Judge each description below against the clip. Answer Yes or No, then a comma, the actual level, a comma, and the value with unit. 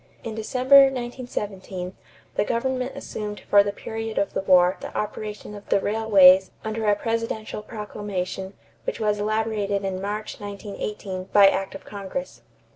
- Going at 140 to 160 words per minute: Yes, average, 145 wpm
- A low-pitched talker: No, high, 210 Hz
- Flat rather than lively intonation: Yes, narrow, 2.2 semitones